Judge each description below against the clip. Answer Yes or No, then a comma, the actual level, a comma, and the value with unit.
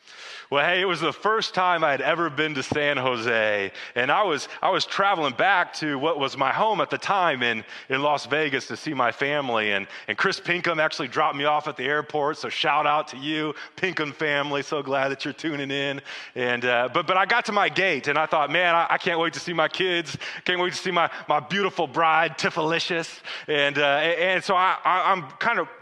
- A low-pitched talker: No, medium, 155 Hz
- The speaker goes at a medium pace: No, fast, 235 wpm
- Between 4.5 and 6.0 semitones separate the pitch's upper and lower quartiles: No, average, 3.3 semitones